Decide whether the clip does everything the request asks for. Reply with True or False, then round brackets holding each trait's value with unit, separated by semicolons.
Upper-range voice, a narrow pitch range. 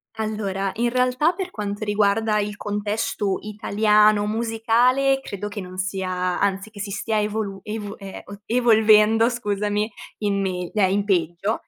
True (210 Hz; 1.8 semitones)